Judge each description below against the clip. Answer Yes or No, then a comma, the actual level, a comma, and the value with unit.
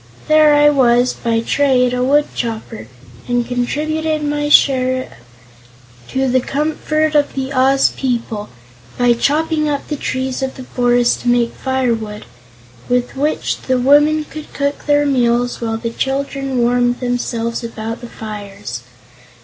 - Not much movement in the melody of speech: No, average, 3.2 semitones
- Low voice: No, very high, 255 Hz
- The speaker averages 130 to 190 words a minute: Yes, average, 140 wpm